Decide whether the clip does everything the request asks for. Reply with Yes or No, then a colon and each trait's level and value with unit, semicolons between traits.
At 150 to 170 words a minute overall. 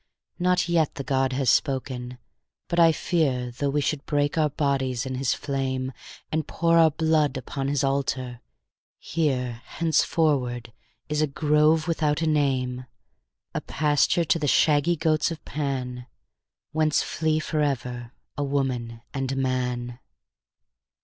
No: average, 140 wpm